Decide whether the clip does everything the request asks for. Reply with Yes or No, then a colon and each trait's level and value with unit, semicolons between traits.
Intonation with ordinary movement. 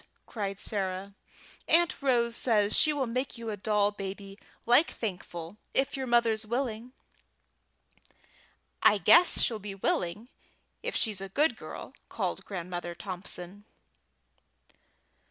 Yes: average, 3.7 semitones